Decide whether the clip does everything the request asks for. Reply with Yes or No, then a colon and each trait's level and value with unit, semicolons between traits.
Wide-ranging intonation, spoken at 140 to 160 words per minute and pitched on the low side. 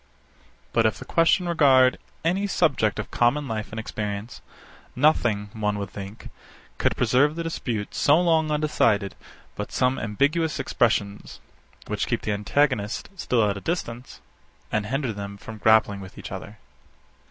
Yes: wide, 6.2 semitones; average, 150 wpm; low, 120 Hz